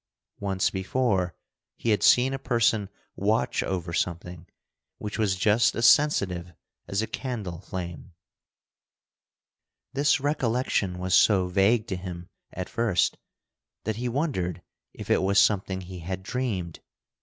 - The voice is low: Yes, low, 100 Hz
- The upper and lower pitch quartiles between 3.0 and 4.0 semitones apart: No, average, 4.4 semitones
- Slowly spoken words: Yes, slow, 130 wpm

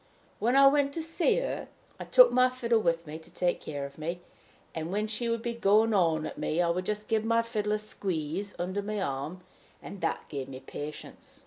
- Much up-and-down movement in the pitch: Yes, wide, 5.9 semitones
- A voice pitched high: Yes, high, 200 Hz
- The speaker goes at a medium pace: No, fast, 220 wpm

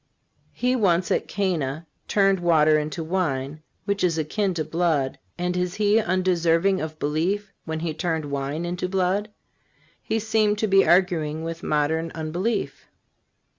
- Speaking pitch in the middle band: Yes, medium, 175 Hz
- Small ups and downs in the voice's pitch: No, average, 3.6 semitones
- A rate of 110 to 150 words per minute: Yes, average, 145 wpm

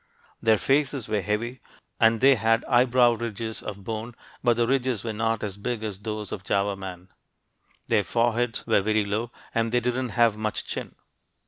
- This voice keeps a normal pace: Yes, average, 180 wpm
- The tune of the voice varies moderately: No, narrow, 2.3 semitones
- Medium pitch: No, low, 115 Hz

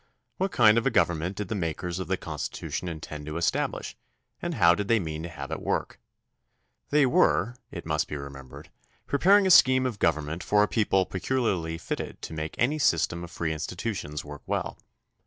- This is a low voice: Yes, very low, 90 Hz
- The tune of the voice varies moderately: No, wide, 6.5 semitones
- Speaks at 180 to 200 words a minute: Yes, average, 190 wpm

